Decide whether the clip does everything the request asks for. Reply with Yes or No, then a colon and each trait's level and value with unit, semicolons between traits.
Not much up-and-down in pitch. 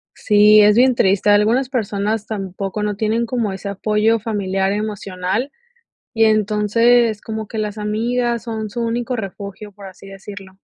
Yes: narrow, 2.2 semitones